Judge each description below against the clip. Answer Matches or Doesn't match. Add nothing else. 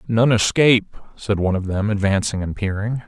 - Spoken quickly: Doesn't match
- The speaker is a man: Matches